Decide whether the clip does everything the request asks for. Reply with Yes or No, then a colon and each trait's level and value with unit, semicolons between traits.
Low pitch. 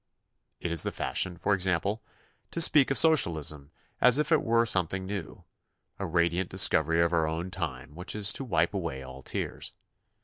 Yes: very low, 90 Hz